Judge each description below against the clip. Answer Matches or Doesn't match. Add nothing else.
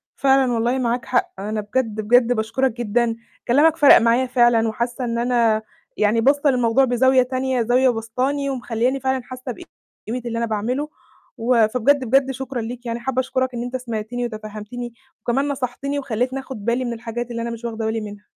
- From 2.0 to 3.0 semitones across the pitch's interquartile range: Matches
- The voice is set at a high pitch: Matches